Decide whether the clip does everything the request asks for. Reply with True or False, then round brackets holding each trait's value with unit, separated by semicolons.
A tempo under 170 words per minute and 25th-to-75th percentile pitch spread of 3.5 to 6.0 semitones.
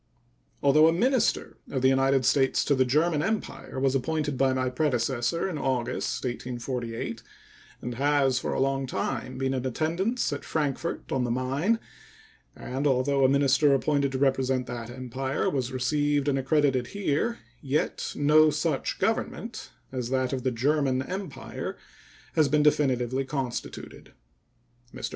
False (150 wpm; 2.5 semitones)